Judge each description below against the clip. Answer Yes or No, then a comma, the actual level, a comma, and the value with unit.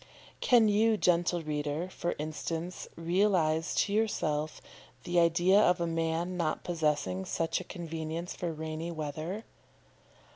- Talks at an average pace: No, slow, 130 wpm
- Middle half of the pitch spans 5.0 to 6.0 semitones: No, narrow, 2.4 semitones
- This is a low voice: No, medium, 170 Hz